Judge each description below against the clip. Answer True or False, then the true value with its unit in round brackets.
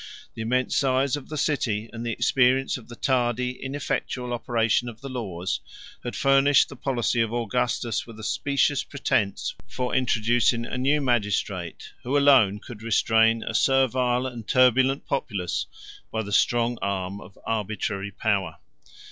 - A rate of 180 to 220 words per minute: False (150 wpm)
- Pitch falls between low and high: False (120 Hz)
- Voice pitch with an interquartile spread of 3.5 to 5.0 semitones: False (3.0 semitones)